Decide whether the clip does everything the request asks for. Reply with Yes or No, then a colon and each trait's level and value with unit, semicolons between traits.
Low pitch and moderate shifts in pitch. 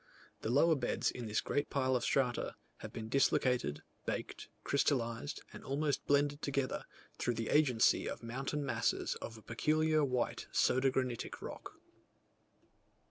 Yes: low, 130 Hz; average, 3.3 semitones